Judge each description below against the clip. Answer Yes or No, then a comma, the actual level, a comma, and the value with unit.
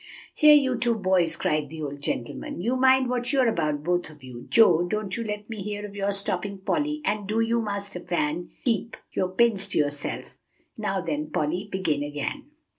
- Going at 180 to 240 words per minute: Yes, average, 190 wpm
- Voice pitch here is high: Yes, high, 200 Hz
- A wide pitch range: Yes, wide, 6.0 semitones